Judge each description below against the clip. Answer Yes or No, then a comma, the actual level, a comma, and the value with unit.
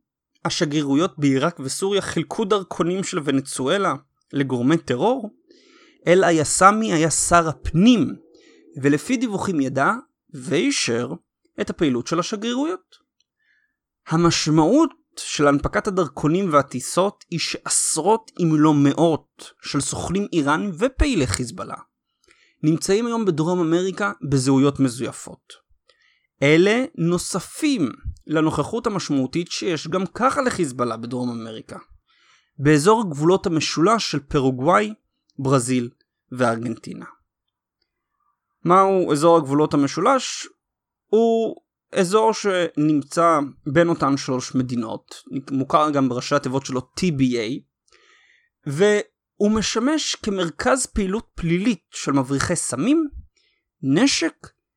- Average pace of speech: No, slow, 95 wpm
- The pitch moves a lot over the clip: Yes, wide, 7.2 semitones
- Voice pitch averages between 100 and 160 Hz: No, medium, 170 Hz